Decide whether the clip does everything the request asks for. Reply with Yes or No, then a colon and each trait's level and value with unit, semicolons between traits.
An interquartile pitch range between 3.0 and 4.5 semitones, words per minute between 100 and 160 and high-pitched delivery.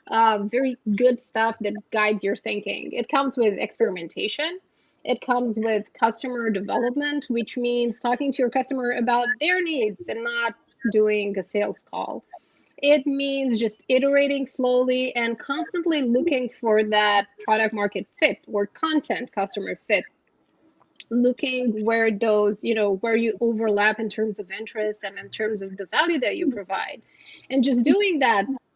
Yes: average, 3.5 semitones; average, 155 wpm; high, 235 Hz